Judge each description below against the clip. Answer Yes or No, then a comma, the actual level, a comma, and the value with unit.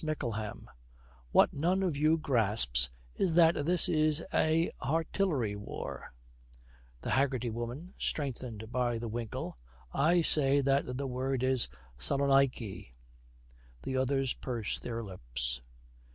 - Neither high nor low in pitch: No, low, 130 Hz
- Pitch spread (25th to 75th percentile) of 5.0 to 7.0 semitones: Yes, wide, 5.6 semitones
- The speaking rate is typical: No, slow, 125 wpm